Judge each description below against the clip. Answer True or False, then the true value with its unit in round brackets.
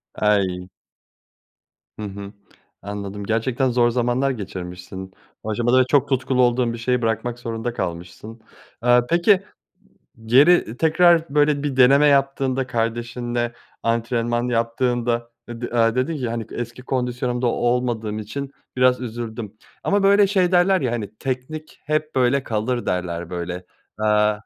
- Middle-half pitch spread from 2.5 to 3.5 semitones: True (3.0 semitones)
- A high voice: False (120 Hz)